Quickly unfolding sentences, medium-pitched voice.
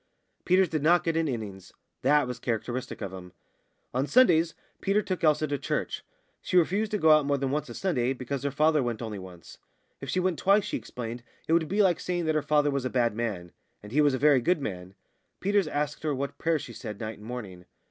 Yes: fast, 230 wpm; medium, 145 Hz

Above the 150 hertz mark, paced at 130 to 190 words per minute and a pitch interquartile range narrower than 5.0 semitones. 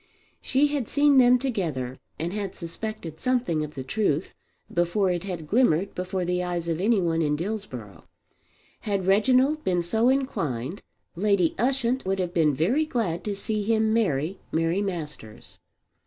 No: high, 190 Hz; average, 155 wpm; wide, 5.5 semitones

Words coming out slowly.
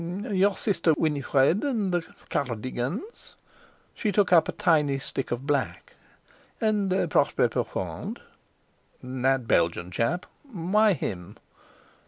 Yes: slow, 110 wpm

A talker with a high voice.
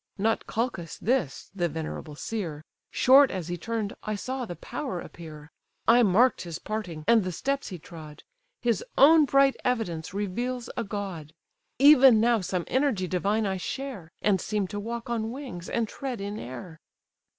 Yes: high, 210 Hz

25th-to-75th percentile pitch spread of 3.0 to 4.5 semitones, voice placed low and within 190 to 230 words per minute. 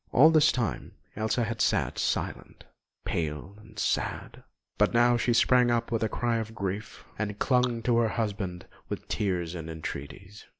No: average, 3.7 semitones; low, 110 Hz; average, 165 wpm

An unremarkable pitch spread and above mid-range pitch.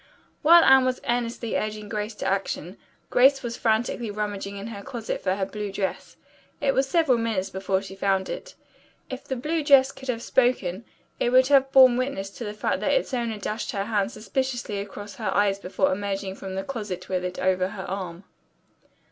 Yes: average, 4.6 semitones; high, 215 Hz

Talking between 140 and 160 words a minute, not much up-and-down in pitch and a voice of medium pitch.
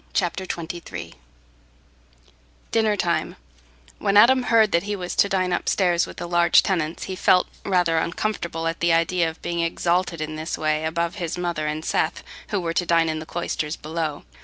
No: average, 180 wpm; narrow, 2.1 semitones; medium, 170 Hz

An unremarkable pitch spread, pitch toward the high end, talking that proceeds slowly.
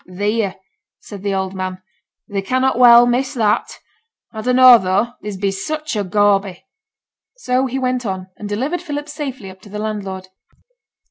No: average, 4.6 semitones; high, 210 Hz; average, 160 wpm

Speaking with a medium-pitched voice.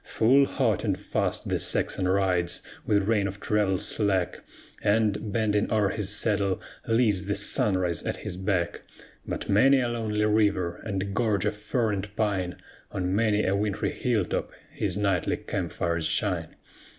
No: low, 100 Hz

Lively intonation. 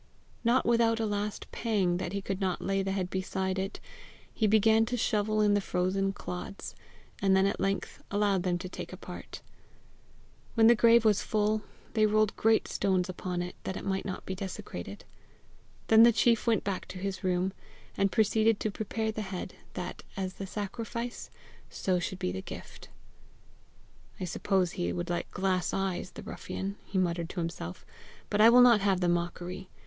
No: average, 2.7 semitones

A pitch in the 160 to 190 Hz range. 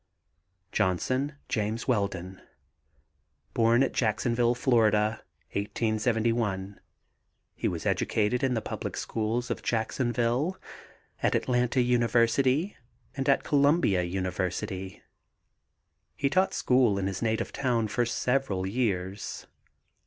No: low, 115 Hz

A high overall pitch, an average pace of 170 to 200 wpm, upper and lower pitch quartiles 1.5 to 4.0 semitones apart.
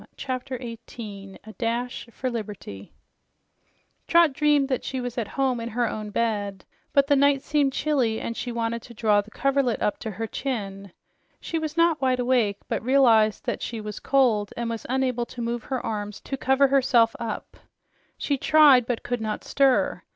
Yes: high, 240 Hz; average, 180 wpm; average, 3.6 semitones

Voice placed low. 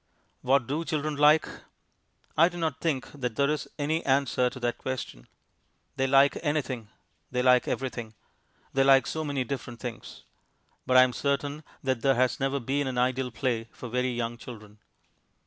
Yes: low, 130 Hz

